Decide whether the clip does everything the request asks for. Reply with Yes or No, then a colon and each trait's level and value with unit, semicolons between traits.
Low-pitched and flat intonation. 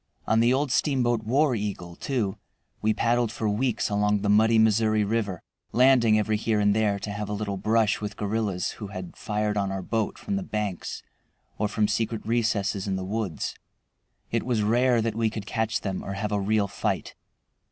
Yes: low, 110 Hz; narrow, 2.0 semitones